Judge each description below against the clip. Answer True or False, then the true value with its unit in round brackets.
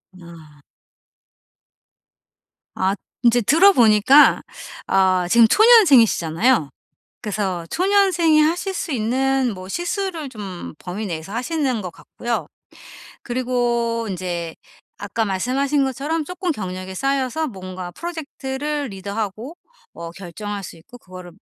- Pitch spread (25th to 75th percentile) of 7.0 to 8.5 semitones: True (7.4 semitones)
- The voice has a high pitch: True (235 Hz)